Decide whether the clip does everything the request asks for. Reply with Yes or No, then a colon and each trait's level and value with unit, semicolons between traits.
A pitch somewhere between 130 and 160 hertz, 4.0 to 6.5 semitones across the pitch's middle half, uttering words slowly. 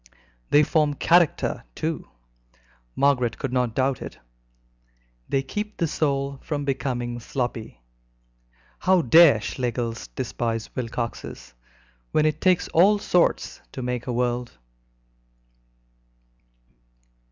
Yes: low, 135 Hz; average, 4.3 semitones; slow, 105 wpm